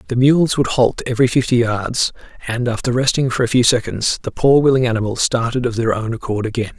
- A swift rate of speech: Yes, fast, 210 wpm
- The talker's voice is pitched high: No, low, 120 Hz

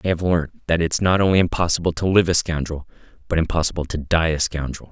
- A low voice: Yes, very low, 80 Hz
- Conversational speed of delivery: No, fast, 220 wpm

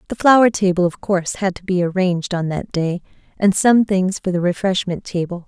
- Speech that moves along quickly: Yes, fast, 210 wpm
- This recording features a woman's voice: Yes, female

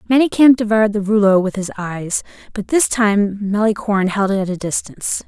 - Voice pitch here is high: Yes, high, 210 Hz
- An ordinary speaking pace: Yes, average, 180 wpm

